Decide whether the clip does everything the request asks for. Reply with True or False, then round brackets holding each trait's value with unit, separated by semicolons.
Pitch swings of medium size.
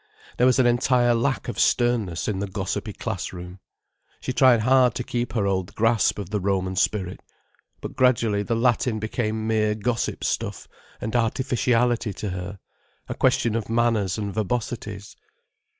True (3.2 semitones)